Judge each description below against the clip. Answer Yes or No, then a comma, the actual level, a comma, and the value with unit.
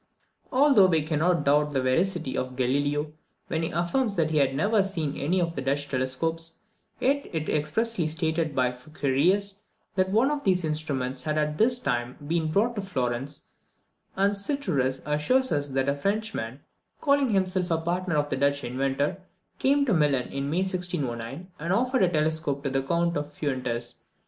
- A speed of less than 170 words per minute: No, average, 180 wpm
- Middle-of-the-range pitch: Yes, medium, 155 Hz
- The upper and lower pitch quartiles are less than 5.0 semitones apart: No, average, 5.3 semitones